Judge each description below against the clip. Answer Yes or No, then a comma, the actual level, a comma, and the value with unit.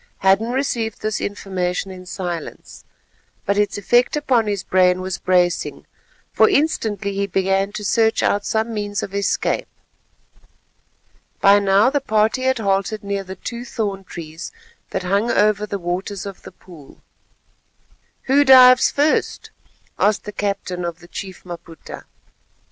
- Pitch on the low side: No, high, 200 Hz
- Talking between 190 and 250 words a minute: No, average, 145 wpm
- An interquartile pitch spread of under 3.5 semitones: Yes, average, 3.0 semitones